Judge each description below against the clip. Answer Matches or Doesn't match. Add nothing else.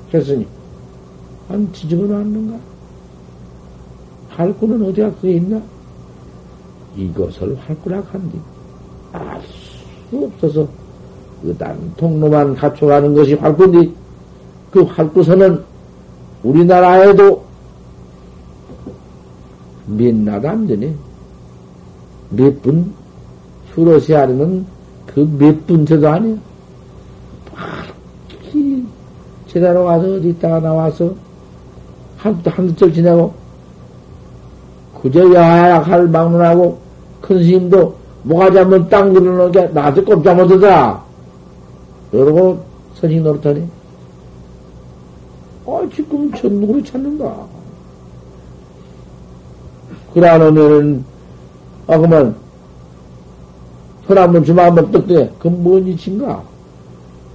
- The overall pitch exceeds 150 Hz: Doesn't match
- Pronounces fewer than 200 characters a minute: Matches